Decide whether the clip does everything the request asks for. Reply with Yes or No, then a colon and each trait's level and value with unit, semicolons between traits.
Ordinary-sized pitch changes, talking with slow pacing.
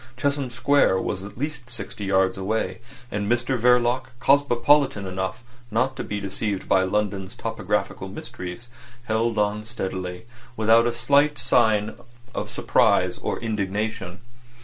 Yes: average, 3.9 semitones; slow, 125 wpm